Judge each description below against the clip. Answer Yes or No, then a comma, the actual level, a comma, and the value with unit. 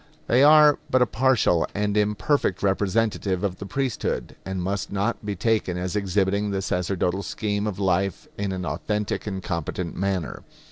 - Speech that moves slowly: No, average, 160 wpm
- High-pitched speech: No, low, 100 Hz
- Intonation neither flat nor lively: No, narrow, 2.3 semitones